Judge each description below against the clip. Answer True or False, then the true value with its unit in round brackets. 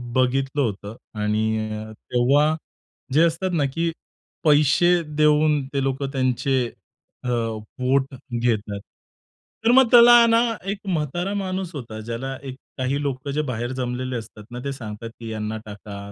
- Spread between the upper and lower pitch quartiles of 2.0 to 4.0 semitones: False (4.7 semitones)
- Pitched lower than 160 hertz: True (135 Hz)